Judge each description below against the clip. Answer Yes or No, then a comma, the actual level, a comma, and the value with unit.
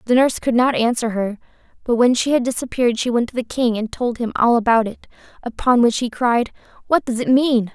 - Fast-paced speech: Yes, fast, 230 wpm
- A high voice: Yes, high, 240 Hz